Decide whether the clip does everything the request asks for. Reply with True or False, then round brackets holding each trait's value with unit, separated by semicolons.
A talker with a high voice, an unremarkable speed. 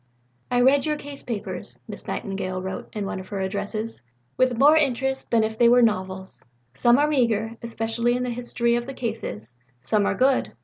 True (235 Hz; 190 wpm)